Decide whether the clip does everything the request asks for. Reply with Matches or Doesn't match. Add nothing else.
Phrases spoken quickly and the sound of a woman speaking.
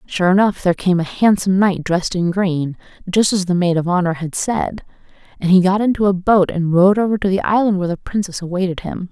Matches